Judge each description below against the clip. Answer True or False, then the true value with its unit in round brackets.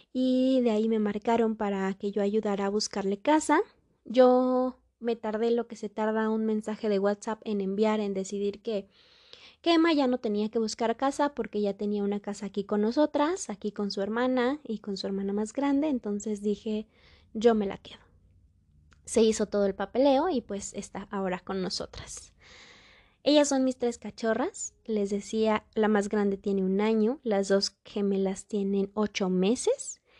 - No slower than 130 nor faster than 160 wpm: False (180 wpm)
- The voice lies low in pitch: False (215 Hz)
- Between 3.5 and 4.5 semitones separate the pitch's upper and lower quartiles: False (3.1 semitones)